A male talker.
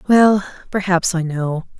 No: female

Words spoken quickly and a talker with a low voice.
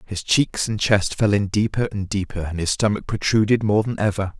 Yes: fast, 220 wpm; low, 105 Hz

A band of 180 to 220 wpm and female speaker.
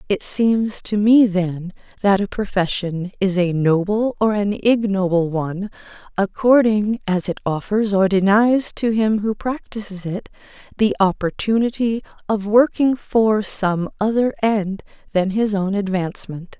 No: slow, 135 wpm; female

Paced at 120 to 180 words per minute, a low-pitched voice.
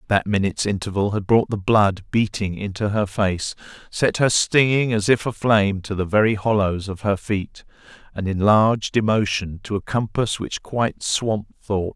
Yes: average, 170 wpm; low, 105 Hz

